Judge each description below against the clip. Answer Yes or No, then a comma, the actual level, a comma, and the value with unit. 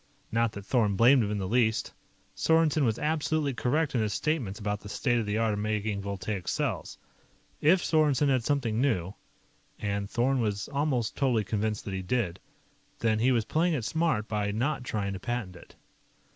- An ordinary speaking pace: Yes, average, 185 wpm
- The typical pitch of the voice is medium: No, low, 115 Hz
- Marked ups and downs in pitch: No, average, 4.8 semitones